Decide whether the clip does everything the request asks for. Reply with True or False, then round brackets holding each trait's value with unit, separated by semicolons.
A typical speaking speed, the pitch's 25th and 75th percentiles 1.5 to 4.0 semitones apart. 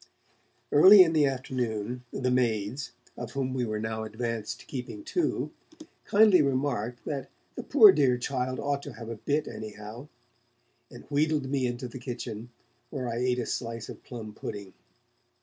True (165 wpm; 3.6 semitones)